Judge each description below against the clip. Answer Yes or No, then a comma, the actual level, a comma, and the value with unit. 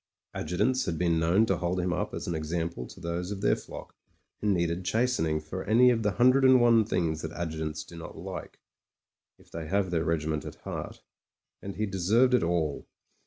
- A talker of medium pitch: No, very low, 90 Hz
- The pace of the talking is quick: Yes, fast, 210 wpm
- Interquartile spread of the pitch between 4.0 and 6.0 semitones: Yes, average, 4.7 semitones